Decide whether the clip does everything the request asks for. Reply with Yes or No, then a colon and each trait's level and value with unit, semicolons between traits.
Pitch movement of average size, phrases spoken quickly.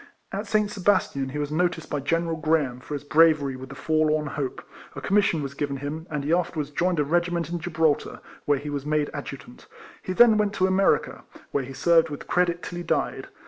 Yes: average, 3.3 semitones; fast, 215 wpm